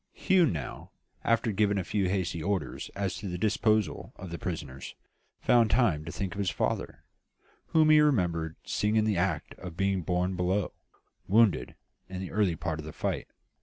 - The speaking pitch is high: No, very low, 95 Hz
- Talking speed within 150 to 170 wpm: No, average, 180 wpm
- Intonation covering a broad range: No, average, 3.7 semitones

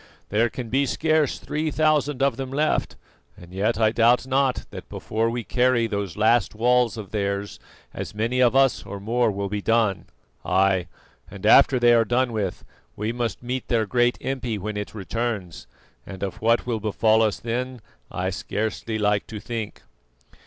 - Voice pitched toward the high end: No, low, 115 Hz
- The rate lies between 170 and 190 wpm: Yes, average, 175 wpm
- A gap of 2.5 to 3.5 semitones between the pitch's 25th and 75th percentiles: Yes, average, 3.2 semitones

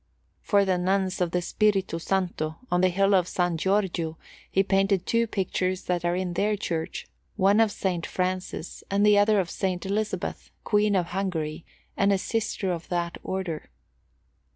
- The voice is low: No, medium, 185 Hz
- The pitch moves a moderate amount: No, narrow, 2.1 semitones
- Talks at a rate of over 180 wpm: No, average, 170 wpm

